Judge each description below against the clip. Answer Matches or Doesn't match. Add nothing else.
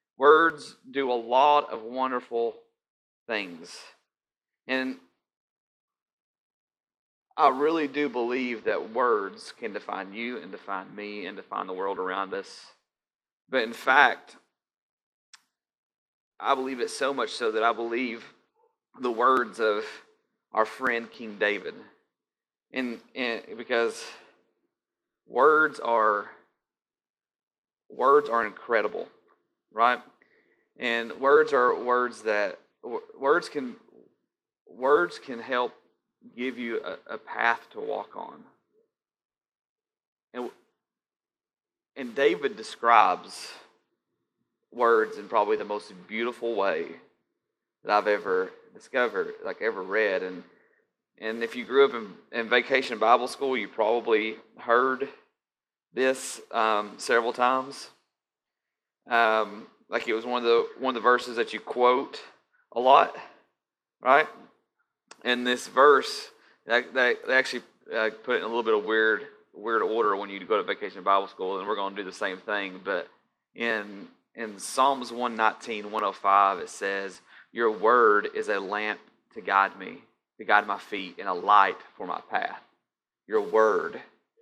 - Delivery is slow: Matches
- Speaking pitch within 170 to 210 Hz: Doesn't match